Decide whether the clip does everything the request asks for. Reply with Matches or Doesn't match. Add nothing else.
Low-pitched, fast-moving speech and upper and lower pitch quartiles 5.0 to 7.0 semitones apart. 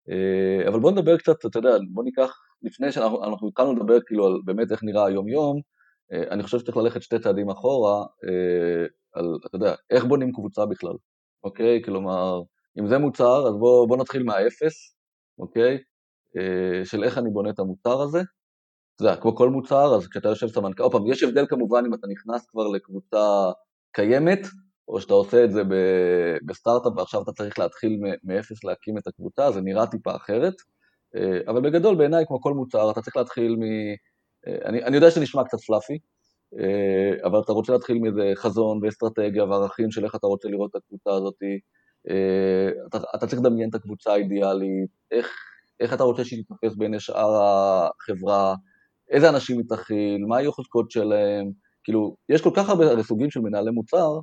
Doesn't match